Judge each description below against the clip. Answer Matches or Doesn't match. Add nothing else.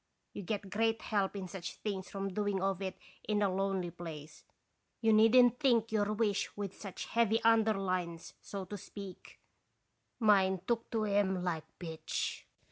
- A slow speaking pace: Doesn't match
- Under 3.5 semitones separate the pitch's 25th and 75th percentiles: Matches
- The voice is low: Doesn't match